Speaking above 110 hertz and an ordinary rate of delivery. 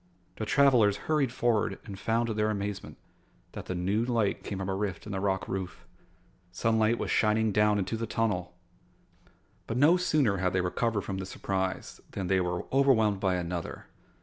No: low, 105 Hz; average, 180 wpm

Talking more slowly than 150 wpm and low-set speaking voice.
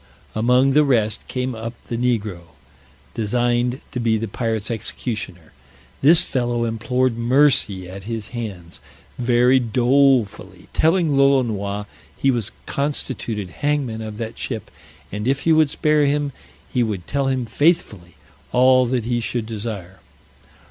Yes: slow, 135 wpm; low, 120 Hz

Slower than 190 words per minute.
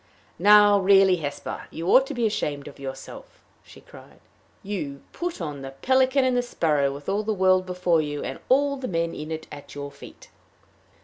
No: average, 195 wpm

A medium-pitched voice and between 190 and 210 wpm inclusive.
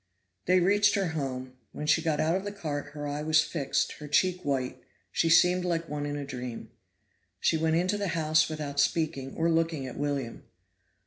Yes: medium, 155 Hz; average, 195 wpm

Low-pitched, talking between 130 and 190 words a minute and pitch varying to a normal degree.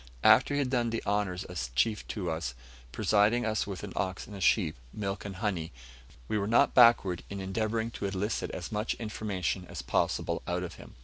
No: low, 100 Hz; average, 200 wpm; average, 3.0 semitones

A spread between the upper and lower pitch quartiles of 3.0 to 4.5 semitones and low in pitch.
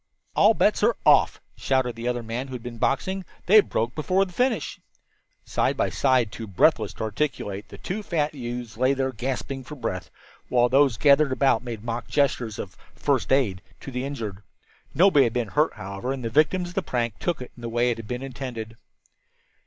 Yes: average, 3.7 semitones; low, 125 Hz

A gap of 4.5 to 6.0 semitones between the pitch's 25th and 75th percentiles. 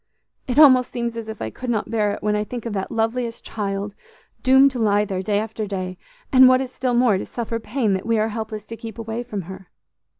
No: average, 2.7 semitones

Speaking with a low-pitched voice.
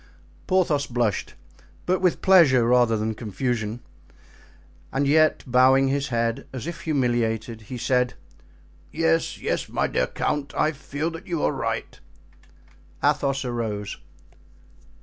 Yes: low, 130 Hz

